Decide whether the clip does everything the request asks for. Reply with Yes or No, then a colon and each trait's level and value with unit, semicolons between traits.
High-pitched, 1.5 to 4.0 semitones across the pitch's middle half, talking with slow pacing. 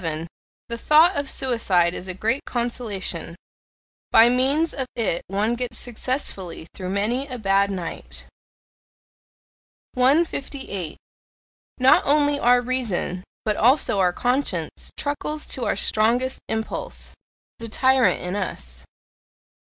No: high, 235 Hz; average, 5.2 semitones; slow, 115 wpm